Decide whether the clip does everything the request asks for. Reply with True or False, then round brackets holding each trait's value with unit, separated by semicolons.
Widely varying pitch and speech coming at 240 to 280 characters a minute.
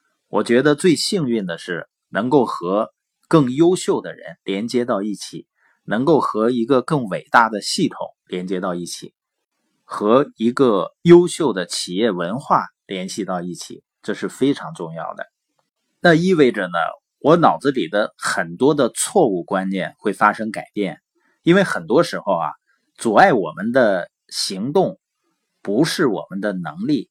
False (8.8 semitones; 225 characters per minute)